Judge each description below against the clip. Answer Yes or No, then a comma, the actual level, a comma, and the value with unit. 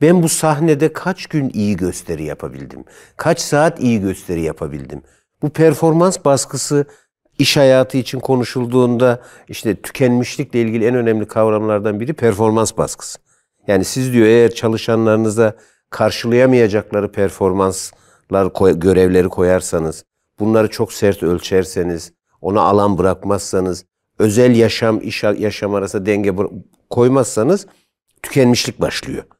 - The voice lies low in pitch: Yes, low, 110 Hz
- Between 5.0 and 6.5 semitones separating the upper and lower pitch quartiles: No, average, 4.6 semitones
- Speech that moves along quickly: No, average, 110 wpm